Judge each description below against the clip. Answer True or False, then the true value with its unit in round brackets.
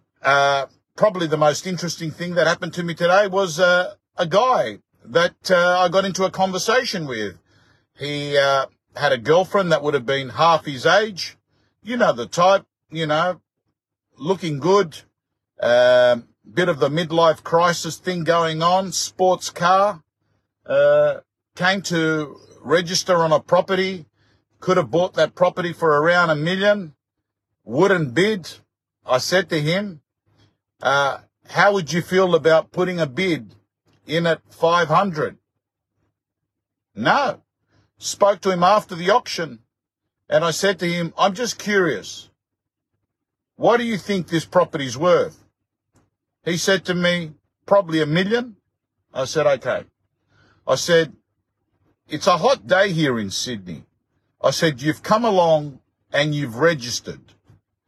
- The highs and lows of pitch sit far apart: True (5.9 semitones)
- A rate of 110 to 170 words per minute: True (140 wpm)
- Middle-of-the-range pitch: True (165 Hz)